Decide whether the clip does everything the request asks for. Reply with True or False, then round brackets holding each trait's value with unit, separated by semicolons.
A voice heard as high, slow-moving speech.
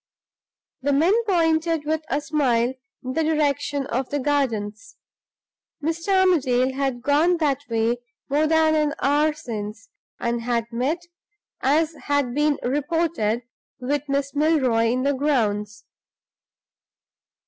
True (285 Hz; 125 wpm)